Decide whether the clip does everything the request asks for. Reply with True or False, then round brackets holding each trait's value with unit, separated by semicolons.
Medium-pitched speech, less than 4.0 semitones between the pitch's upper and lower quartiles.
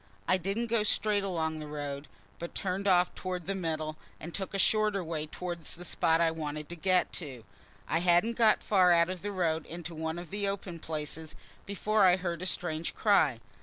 True (175 Hz; 3.5 semitones)